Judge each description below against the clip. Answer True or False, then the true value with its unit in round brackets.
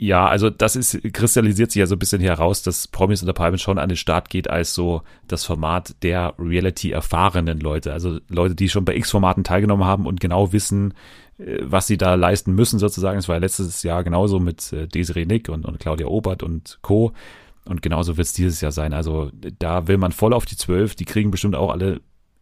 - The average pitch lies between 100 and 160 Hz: False (90 Hz)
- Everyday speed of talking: False (210 wpm)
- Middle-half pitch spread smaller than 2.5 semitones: False (2.9 semitones)